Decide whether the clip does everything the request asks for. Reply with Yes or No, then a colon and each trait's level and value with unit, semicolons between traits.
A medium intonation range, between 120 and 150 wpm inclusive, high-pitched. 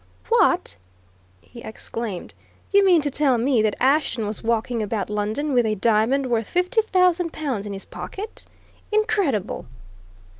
No: wide, 7.4 semitones; average, 145 wpm; very high, 250 Hz